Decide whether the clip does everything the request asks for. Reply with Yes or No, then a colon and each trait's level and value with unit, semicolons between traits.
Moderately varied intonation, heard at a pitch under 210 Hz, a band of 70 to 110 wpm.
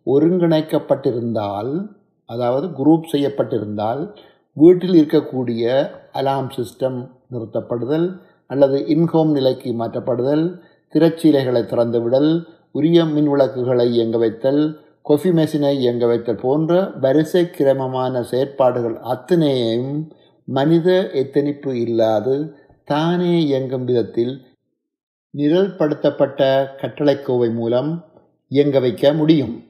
Yes: average, 4.2 semitones; medium, 140 Hz; average, 80 wpm